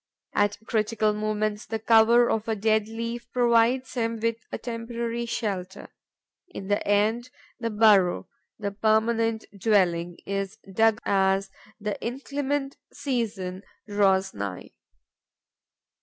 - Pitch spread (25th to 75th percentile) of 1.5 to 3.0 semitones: Yes, narrow, 2.4 semitones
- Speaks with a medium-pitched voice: No, high, 220 Hz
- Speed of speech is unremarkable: No, slow, 115 wpm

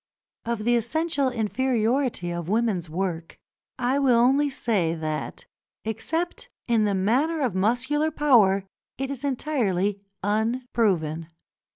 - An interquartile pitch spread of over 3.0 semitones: Yes, wide, 5.6 semitones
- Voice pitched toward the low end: No, high, 230 Hz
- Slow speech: Yes, slow, 115 wpm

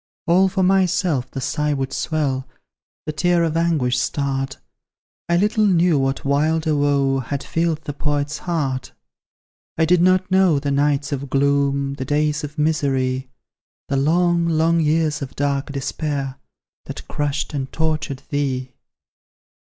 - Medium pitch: Yes, medium, 145 Hz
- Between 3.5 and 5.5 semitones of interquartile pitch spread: No, average, 3.1 semitones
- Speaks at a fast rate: No, average, 145 wpm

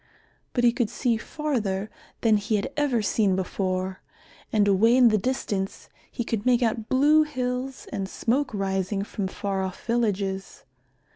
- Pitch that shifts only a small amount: No, average, 4.2 semitones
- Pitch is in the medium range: No, high, 220 Hz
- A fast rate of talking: No, average, 155 wpm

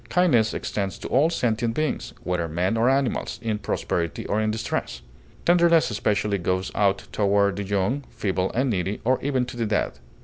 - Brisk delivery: No, average, 175 wpm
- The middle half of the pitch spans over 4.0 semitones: Yes, average, 4.7 semitones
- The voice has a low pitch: Yes, low, 110 Hz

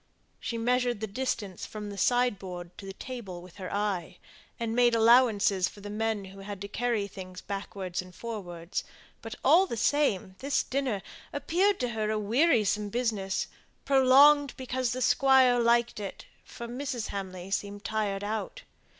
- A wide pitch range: No, average, 4.1 semitones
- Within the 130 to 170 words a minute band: Yes, average, 160 wpm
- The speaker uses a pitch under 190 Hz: No, high, 220 Hz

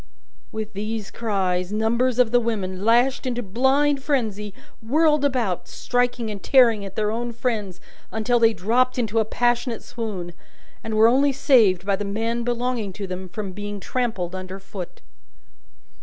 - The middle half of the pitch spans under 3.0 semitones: No, average, 3.6 semitones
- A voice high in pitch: Yes, high, 225 Hz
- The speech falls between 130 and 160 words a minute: Yes, average, 155 wpm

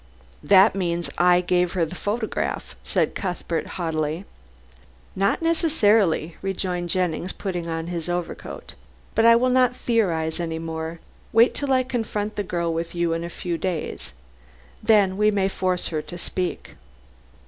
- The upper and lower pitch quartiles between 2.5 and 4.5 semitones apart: Yes, average, 3.8 semitones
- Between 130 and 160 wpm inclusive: Yes, average, 150 wpm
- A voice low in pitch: No, medium, 180 Hz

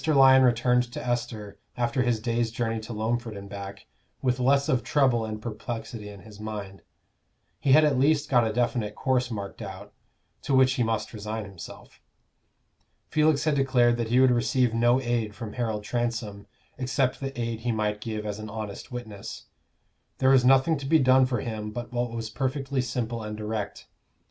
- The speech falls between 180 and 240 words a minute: Yes, average, 185 wpm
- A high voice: No, low, 120 Hz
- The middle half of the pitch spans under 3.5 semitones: Yes, average, 3.0 semitones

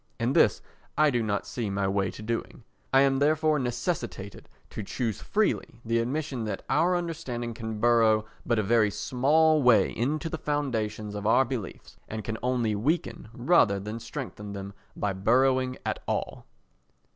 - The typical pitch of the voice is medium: No, low, 120 Hz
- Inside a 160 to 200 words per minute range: Yes, average, 165 wpm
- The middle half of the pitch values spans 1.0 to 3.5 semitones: No, average, 4.3 semitones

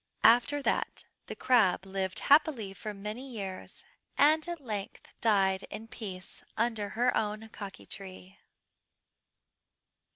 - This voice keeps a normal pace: No, slow, 120 wpm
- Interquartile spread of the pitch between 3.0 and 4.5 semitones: Yes, average, 4.0 semitones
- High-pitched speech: Yes, high, 215 Hz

